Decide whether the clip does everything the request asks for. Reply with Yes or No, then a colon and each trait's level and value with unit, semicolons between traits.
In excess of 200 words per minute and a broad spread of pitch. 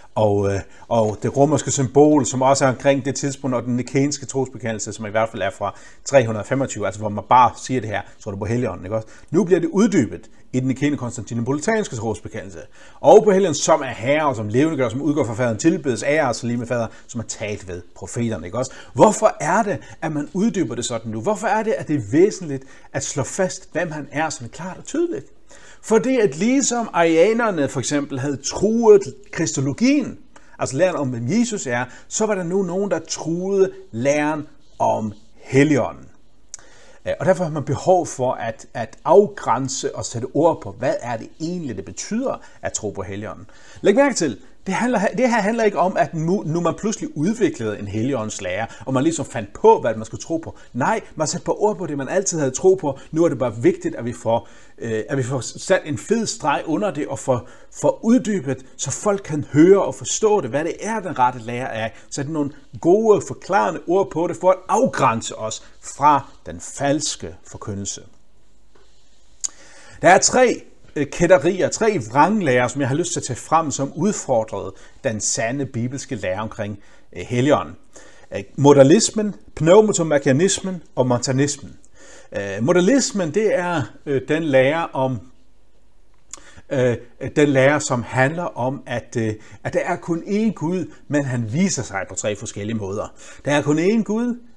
No: average, 185 wpm; wide, 7.1 semitones